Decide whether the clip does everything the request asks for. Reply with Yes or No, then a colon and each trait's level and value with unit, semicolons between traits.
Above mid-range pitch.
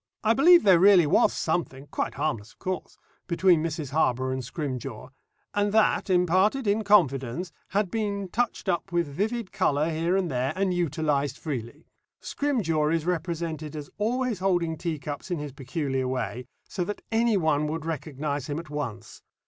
No: medium, 165 Hz